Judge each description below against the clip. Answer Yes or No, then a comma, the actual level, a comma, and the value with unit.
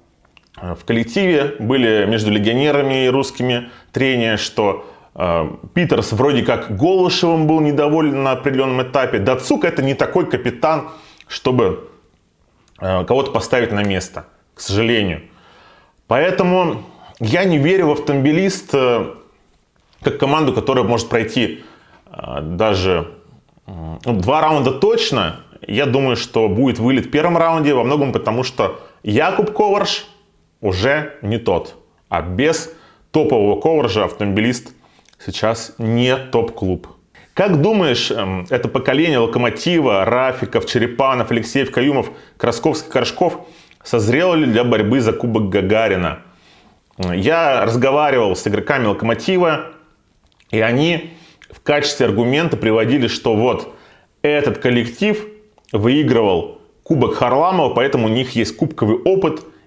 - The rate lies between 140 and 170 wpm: No, average, 120 wpm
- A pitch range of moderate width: No, wide, 5.9 semitones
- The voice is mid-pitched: No, low, 130 Hz